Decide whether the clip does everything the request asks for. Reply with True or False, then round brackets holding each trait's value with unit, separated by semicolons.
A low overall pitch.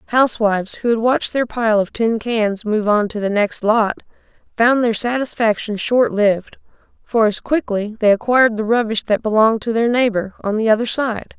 False (225 Hz)